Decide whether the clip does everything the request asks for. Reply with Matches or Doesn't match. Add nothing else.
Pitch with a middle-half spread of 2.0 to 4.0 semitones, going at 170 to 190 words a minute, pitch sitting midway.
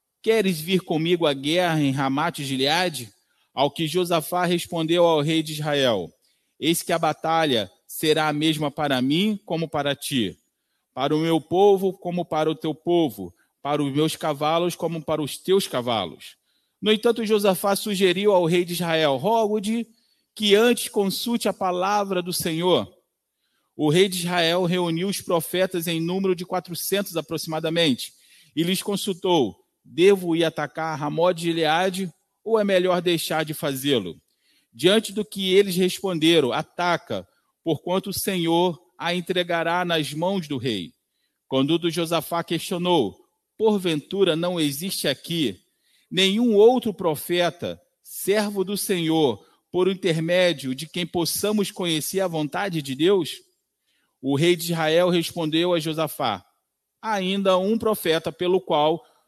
Doesn't match